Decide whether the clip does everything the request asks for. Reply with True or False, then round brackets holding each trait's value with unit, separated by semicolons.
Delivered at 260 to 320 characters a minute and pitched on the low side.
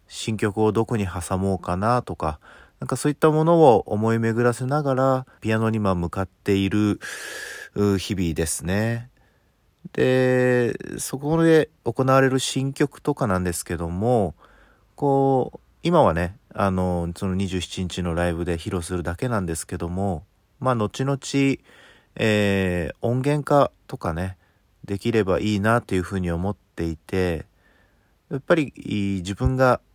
True (265 characters per minute; 105 Hz)